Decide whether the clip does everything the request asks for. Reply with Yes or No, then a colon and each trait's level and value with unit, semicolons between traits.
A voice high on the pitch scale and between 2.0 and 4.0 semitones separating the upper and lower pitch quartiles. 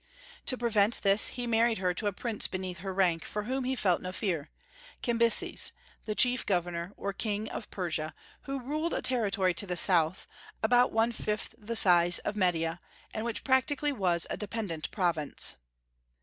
No: high, 205 Hz; average, 4.7 semitones